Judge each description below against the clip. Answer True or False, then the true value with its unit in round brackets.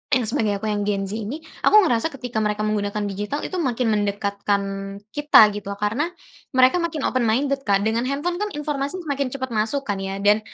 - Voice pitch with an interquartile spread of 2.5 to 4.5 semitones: False (5.2 semitones)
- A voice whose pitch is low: False (230 Hz)